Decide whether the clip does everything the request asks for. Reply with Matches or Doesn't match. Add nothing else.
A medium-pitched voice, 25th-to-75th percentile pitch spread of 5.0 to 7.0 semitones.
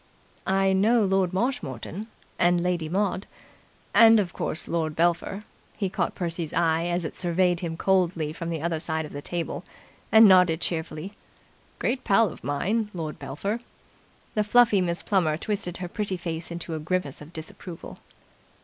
Doesn't match